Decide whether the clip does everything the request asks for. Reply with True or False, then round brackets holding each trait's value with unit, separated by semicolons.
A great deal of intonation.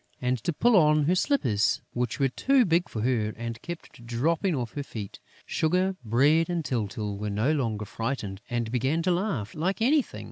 True (7.1 semitones)